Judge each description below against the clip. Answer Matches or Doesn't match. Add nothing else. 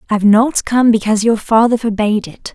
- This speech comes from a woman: Matches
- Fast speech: Doesn't match